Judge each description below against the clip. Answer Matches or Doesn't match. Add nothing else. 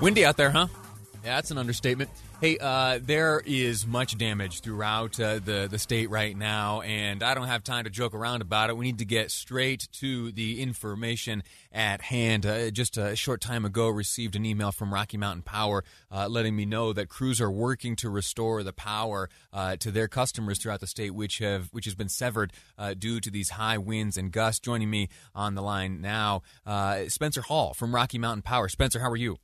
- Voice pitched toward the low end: Matches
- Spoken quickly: Matches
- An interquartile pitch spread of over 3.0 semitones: Doesn't match